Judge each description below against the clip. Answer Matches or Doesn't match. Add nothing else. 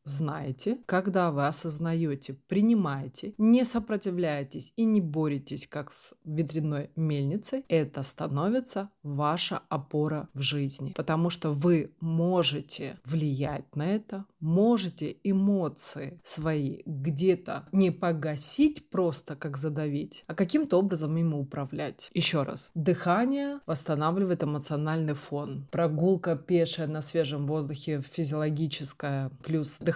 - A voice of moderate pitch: Matches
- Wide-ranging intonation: Doesn't match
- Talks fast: Doesn't match